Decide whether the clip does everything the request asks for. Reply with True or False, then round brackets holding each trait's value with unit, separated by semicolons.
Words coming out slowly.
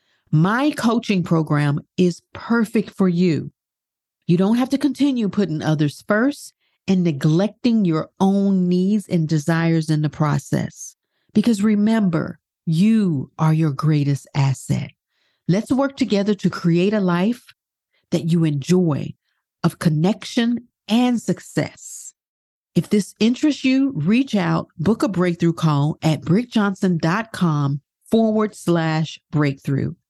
True (120 wpm)